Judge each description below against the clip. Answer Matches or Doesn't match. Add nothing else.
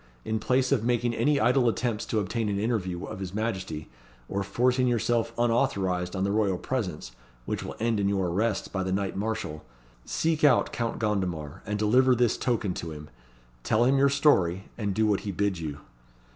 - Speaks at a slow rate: Doesn't match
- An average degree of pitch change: Matches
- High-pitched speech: Doesn't match